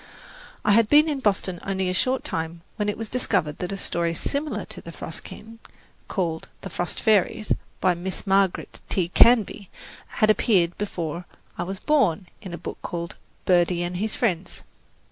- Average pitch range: Yes, average, 3.7 semitones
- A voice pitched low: No, high, 190 Hz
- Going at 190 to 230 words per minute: No, average, 175 wpm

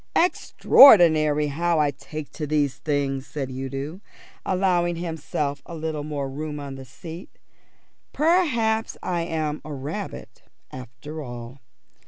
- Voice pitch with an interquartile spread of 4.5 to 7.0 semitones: No, average, 3.7 semitones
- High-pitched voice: No, medium, 150 Hz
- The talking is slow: Yes, slow, 125 wpm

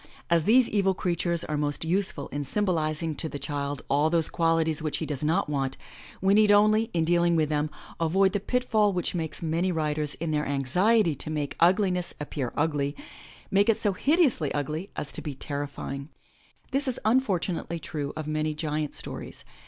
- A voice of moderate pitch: Yes, medium, 160 Hz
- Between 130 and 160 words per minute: No, average, 185 wpm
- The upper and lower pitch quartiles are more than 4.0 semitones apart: Yes, average, 4.4 semitones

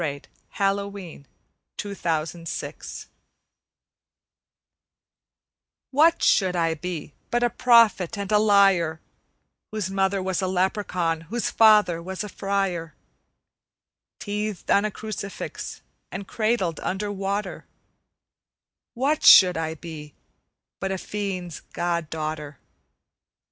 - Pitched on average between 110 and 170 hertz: No, high, 190 Hz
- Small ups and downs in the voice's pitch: No, average, 3.7 semitones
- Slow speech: Yes, slow, 110 wpm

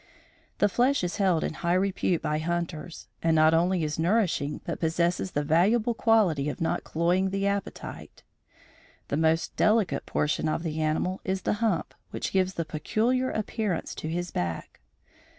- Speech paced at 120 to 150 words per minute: No, average, 165 wpm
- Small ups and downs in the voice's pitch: No, average, 3.8 semitones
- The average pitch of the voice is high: No, medium, 175 Hz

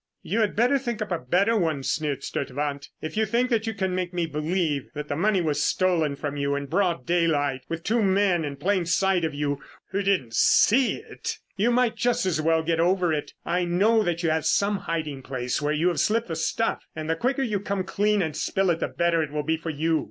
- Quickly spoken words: Yes, fast, 235 wpm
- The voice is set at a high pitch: No, medium, 170 Hz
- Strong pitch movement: No, average, 4.9 semitones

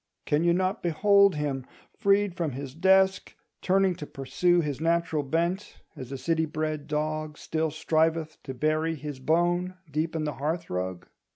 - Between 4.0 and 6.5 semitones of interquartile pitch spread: No, average, 2.8 semitones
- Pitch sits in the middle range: Yes, medium, 160 Hz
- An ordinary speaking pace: Yes, average, 165 wpm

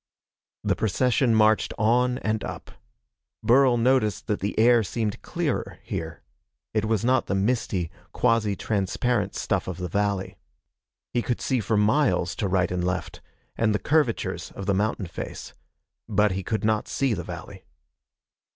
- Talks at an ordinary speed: Yes, average, 155 wpm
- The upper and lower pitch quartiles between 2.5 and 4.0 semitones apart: Yes, average, 3.6 semitones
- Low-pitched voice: Yes, low, 110 Hz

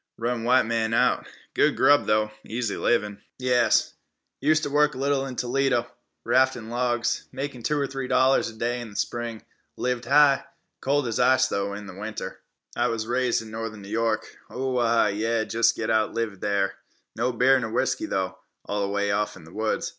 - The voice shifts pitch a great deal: No, average, 3.0 semitones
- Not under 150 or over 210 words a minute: Yes, average, 180 wpm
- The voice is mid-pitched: No, low, 115 Hz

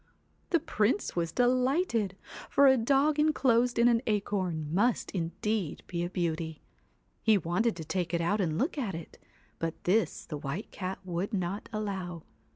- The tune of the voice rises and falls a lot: Yes, wide, 5.7 semitones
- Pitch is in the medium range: No, high, 200 Hz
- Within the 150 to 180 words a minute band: Yes, average, 160 wpm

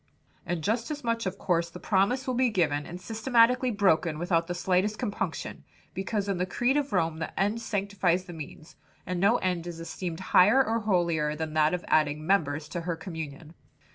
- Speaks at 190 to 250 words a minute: Yes, average, 195 wpm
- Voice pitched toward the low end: No, medium, 180 Hz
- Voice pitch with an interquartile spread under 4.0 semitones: No, average, 4.5 semitones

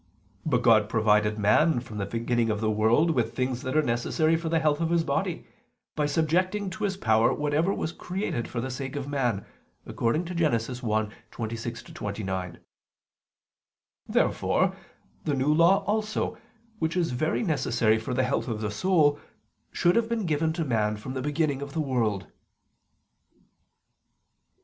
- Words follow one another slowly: No, average, 155 wpm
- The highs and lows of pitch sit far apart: Yes, wide, 6.3 semitones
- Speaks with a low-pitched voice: Yes, low, 130 Hz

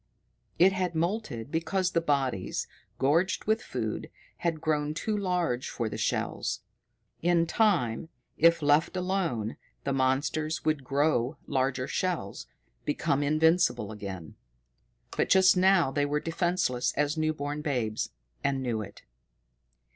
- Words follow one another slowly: Yes, slow, 130 wpm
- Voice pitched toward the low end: No, medium, 150 Hz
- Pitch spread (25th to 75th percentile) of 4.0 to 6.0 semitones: Yes, average, 4.8 semitones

